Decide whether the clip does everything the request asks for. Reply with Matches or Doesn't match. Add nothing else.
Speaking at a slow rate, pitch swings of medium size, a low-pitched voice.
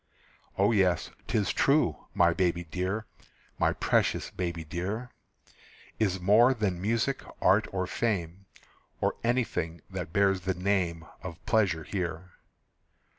Matches